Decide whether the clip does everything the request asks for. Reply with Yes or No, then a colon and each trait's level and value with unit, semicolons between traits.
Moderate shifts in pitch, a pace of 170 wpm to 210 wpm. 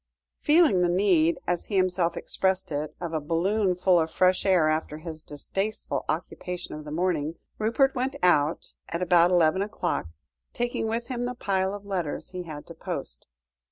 Yes: average, 3.6 semitones; average, 175 wpm